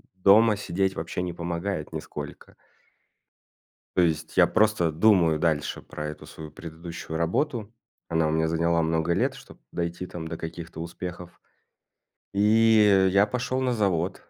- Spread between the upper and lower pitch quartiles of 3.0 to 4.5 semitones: Yes, average, 3.7 semitones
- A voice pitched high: No, very low, 85 Hz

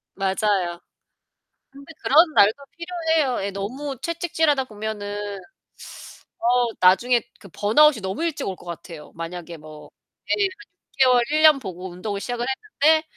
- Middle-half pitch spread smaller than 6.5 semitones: No, wide, 7.8 semitones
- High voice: Yes, high, 220 Hz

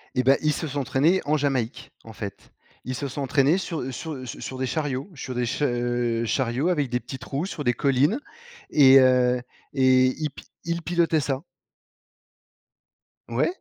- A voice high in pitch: No, low, 135 Hz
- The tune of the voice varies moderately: Yes, average, 3.1 semitones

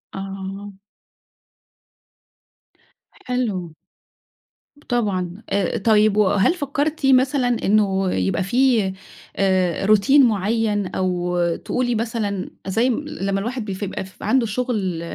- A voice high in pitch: Yes, high, 205 Hz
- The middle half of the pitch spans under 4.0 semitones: No, average, 4.3 semitones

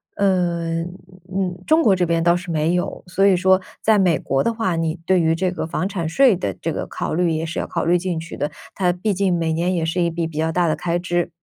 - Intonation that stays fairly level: Yes, narrow, 2.1 semitones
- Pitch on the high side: No, medium, 175 Hz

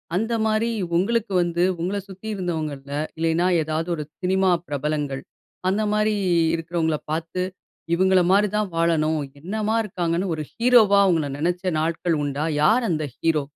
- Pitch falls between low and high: Yes, medium, 175 Hz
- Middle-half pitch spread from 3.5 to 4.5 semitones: Yes, average, 4.1 semitones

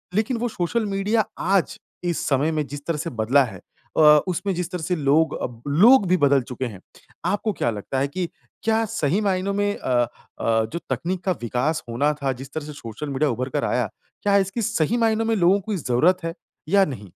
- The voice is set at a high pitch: No, medium, 160 Hz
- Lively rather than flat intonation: Yes, wide, 6.5 semitones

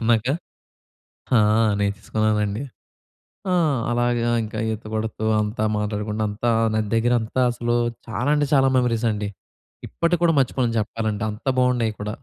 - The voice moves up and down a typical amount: No, narrow, 2.3 semitones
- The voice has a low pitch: Yes, low, 115 Hz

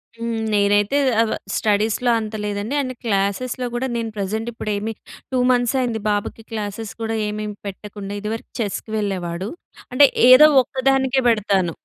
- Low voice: No, high, 220 Hz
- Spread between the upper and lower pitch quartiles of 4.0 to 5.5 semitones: No, average, 2.9 semitones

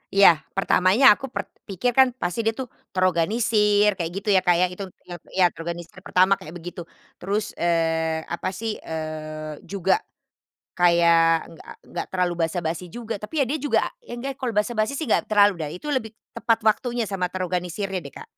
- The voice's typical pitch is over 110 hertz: Yes, medium, 185 Hz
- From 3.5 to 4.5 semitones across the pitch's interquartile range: Yes, average, 4.2 semitones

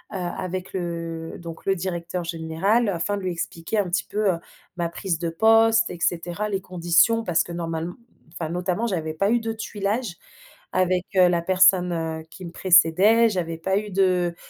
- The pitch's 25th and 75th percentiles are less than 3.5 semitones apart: Yes, average, 2.8 semitones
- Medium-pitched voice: Yes, medium, 180 Hz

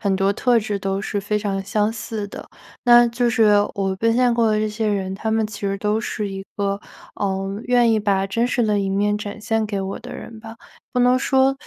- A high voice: Yes, high, 210 Hz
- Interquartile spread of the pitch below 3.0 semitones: Yes, narrow, 2.4 semitones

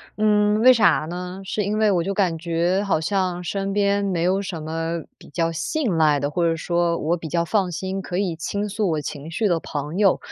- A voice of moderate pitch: Yes, medium, 180 Hz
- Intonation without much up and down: No, average, 3.3 semitones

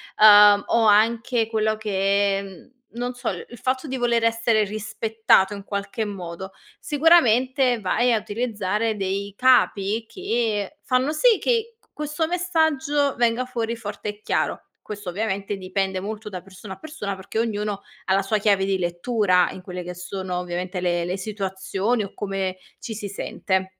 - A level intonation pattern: No, average, 3.8 semitones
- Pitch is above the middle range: Yes, high, 210 Hz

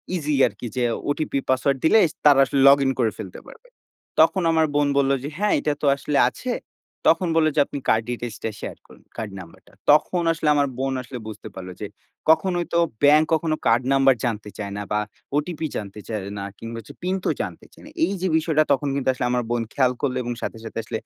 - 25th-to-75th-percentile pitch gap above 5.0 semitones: Yes, wide, 5.4 semitones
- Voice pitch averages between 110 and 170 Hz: Yes, low, 135 Hz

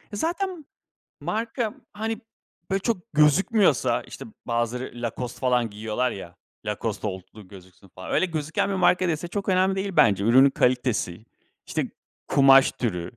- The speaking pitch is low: Yes, low, 130 Hz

